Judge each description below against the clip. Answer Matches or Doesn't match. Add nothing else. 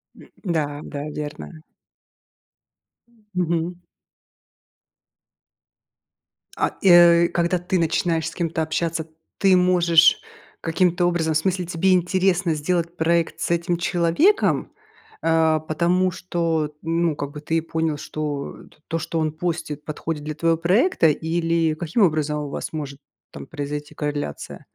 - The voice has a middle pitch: Matches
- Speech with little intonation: Matches